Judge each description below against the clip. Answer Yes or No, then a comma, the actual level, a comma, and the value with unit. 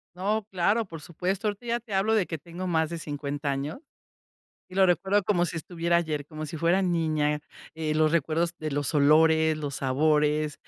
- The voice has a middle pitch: Yes, medium, 160 Hz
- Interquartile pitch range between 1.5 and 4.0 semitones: Yes, average, 3.5 semitones